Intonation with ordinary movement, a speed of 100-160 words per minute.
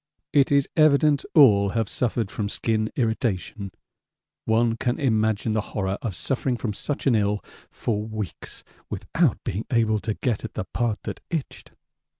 Yes: average, 3.1 semitones; average, 155 wpm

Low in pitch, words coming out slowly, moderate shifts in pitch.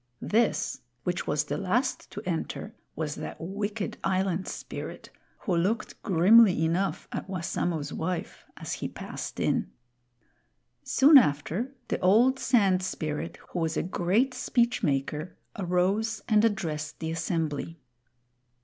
No: medium, 185 Hz; slow, 130 wpm; average, 4.8 semitones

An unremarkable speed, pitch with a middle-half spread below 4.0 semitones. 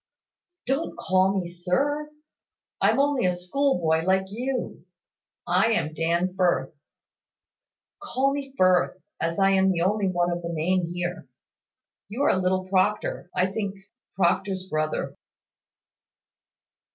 No: slow, 125 wpm; average, 3.3 semitones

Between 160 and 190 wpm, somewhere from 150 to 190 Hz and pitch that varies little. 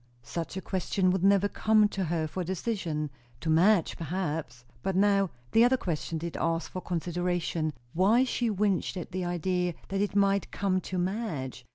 No: average, 175 wpm; medium, 185 Hz; average, 3.1 semitones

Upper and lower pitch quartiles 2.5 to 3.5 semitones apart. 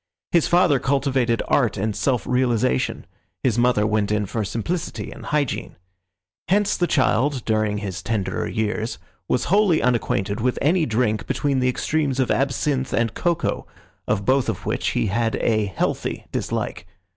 No: average, 4.6 semitones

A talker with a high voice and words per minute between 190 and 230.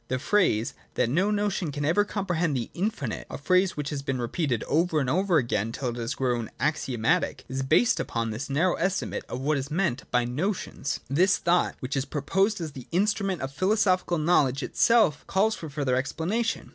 No: medium, 150 Hz; average, 195 wpm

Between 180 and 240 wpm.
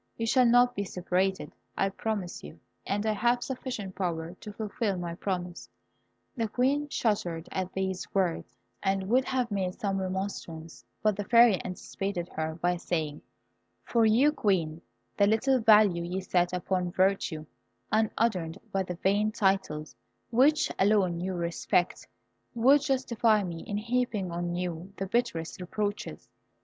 No: average, 145 wpm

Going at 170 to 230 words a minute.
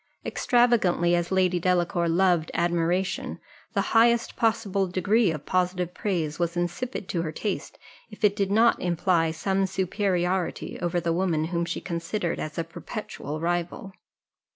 No: average, 145 wpm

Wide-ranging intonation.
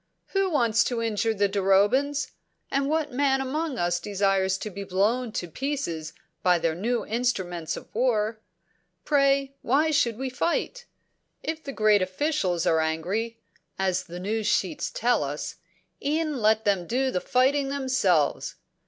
Yes: wide, 6.3 semitones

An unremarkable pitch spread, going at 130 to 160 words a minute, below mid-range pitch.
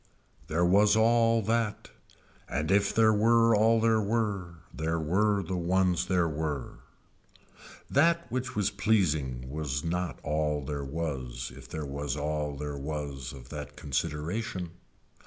No: wide, 6.3 semitones; average, 140 wpm; very low, 85 Hz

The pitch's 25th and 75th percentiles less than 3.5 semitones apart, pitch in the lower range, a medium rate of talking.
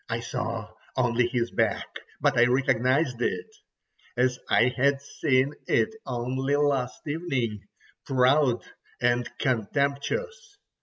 No: narrow, 2.6 semitones; low, 130 Hz; slow, 110 wpm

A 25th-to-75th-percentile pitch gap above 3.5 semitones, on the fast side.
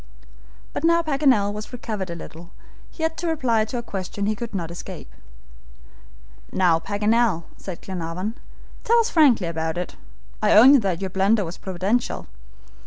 No: average, 5.3 semitones; average, 165 wpm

